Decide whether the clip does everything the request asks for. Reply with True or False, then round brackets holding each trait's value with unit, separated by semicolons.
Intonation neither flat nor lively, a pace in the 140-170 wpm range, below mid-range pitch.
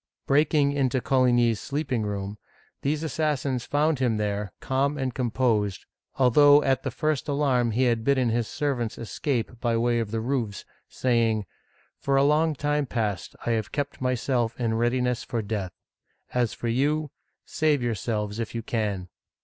True (3.8 semitones; 160 wpm; 125 Hz)